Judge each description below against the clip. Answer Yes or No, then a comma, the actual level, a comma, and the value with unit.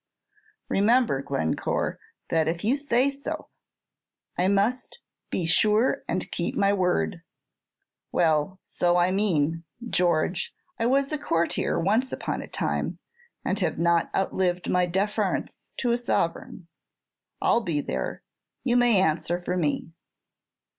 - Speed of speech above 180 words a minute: No, slow, 135 wpm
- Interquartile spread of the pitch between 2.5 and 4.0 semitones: No, wide, 5.4 semitones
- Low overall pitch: No, medium, 180 Hz